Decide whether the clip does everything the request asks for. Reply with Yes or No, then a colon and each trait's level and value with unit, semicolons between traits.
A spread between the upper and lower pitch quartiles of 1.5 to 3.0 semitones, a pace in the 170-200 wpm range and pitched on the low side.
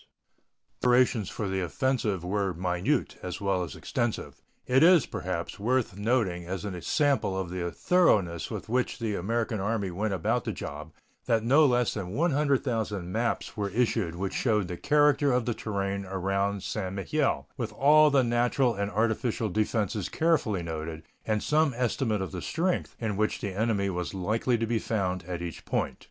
No: average, 4.6 semitones; average, 175 wpm; low, 105 Hz